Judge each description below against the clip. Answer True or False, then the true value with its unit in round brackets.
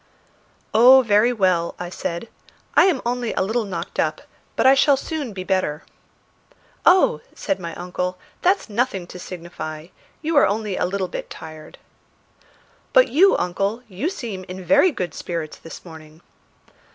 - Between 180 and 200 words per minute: False (155 wpm)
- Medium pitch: False (195 Hz)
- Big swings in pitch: True (6.3 semitones)